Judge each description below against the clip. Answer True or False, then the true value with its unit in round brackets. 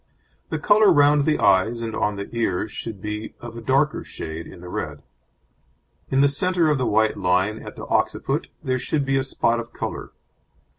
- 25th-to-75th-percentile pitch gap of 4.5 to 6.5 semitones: True (5.3 semitones)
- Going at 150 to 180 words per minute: False (195 wpm)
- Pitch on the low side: True (115 Hz)